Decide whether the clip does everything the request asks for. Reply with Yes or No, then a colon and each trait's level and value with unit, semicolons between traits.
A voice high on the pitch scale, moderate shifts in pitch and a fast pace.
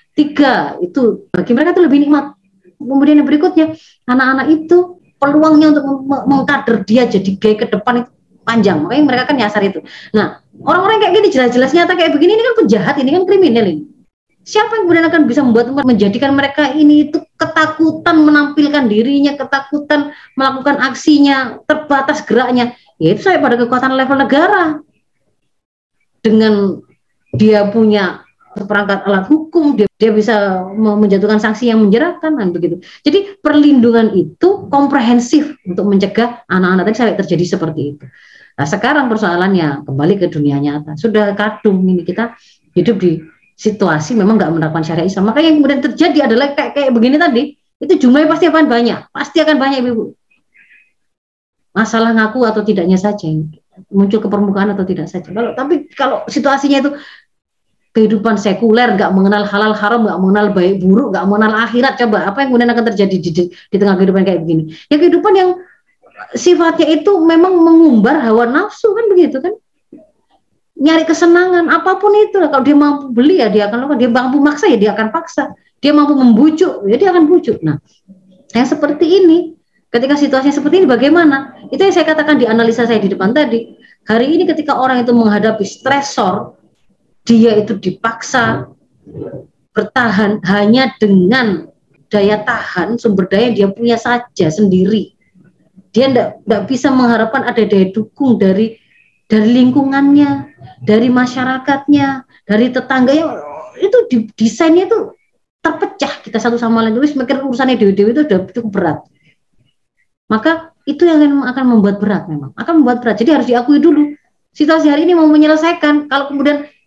No: very high, 250 Hz; wide, 6.0 semitones; fast, 160 wpm